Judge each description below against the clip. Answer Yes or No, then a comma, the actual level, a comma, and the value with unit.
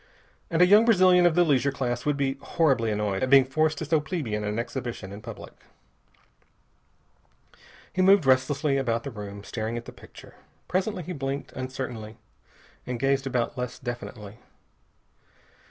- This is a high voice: No, low, 130 Hz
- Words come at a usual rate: Yes, average, 155 wpm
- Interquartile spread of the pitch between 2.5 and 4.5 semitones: No, average, 4.9 semitones